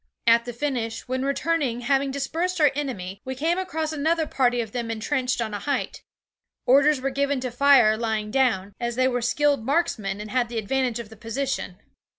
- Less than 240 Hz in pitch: No, very high, 255 Hz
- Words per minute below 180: No, average, 190 wpm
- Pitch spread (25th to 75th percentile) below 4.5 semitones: Yes, average, 3.7 semitones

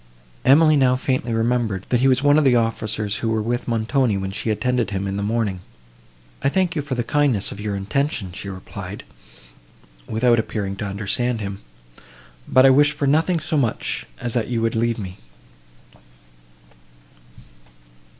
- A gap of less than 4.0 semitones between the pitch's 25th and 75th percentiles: No, average, 4.4 semitones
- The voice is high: No, low, 115 Hz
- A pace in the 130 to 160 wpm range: No, average, 170 wpm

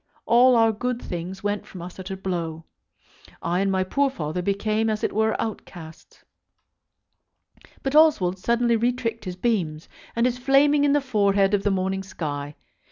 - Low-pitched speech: No, high, 205 Hz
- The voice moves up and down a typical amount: Yes, average, 4.5 semitones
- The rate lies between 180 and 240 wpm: No, average, 165 wpm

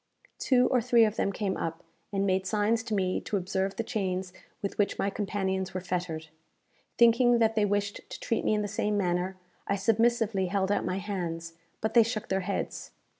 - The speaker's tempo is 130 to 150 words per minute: No, average, 200 wpm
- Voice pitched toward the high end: Yes, high, 200 Hz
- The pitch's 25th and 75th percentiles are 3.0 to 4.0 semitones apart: No, narrow, 2.6 semitones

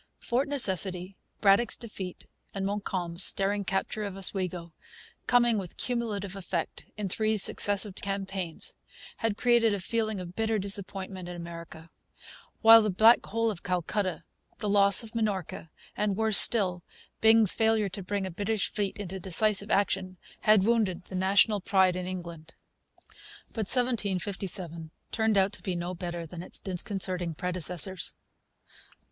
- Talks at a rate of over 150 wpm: No, average, 140 wpm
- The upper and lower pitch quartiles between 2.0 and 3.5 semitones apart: Yes, average, 2.8 semitones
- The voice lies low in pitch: No, high, 195 Hz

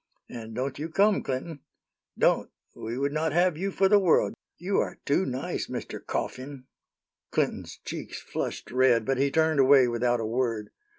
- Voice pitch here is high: No, low, 135 Hz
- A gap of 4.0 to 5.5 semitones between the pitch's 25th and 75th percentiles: Yes, average, 4.6 semitones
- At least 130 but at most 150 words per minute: No, average, 170 wpm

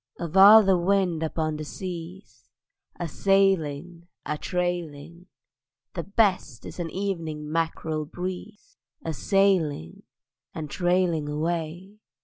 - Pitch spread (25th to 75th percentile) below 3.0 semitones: No, average, 3.3 semitones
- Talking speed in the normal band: No, slow, 115 wpm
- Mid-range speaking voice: Yes, medium, 170 Hz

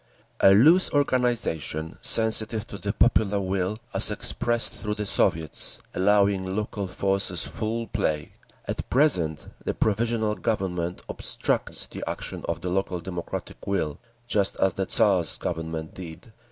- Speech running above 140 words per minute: No, slow, 135 wpm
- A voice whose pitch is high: No, low, 100 Hz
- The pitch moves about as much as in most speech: Yes, average, 3.8 semitones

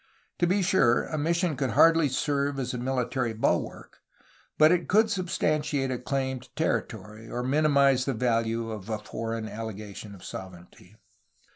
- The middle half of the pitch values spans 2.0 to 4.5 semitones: No, average, 5.2 semitones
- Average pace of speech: Yes, average, 160 wpm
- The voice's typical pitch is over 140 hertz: No, low, 130 Hz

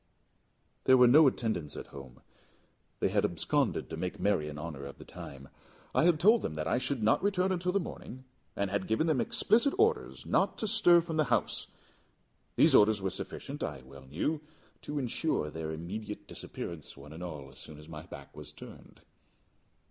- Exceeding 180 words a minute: Yes, average, 190 wpm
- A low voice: Yes, low, 105 Hz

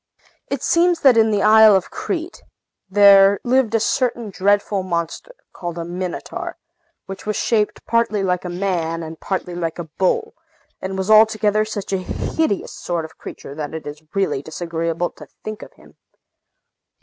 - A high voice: Yes, high, 195 Hz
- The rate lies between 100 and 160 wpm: No, average, 170 wpm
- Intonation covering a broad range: No, average, 3.9 semitones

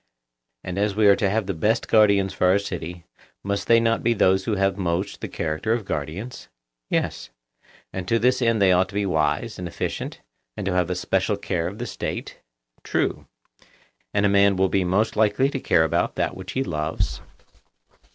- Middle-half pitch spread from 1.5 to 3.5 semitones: Yes, average, 2.9 semitones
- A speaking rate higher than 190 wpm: Yes, average, 200 wpm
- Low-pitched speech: Yes, low, 100 Hz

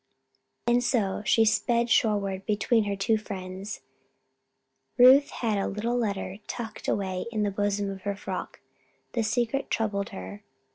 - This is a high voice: Yes, high, 210 Hz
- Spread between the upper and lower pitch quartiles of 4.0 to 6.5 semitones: No, average, 2.8 semitones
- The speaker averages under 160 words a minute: Yes, average, 150 wpm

